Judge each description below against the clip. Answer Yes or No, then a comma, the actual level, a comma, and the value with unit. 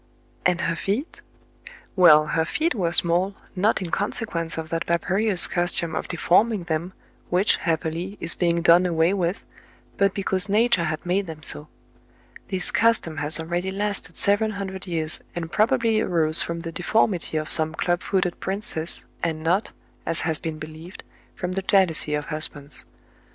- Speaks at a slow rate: No, average, 160 wpm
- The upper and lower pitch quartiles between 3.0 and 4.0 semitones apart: Yes, average, 3.3 semitones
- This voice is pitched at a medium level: Yes, medium, 175 Hz